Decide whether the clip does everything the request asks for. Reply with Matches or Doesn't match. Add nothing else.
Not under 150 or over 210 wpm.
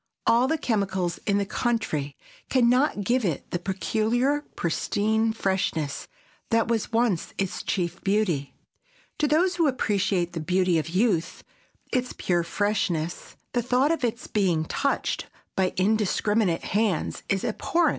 Doesn't match